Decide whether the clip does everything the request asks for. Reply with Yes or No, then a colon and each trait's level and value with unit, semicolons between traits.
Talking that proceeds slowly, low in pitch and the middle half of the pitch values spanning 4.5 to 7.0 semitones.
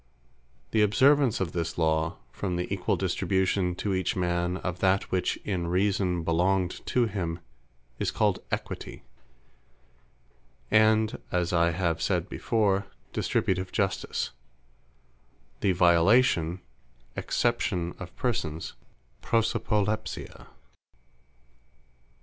No: slow, 100 wpm; very low, 95 Hz; average, 3.1 semitones